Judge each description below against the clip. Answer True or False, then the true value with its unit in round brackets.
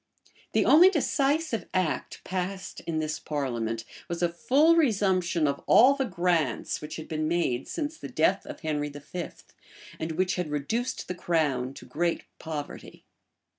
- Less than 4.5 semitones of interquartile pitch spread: False (5.1 semitones)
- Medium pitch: True (170 Hz)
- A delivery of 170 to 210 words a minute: False (155 wpm)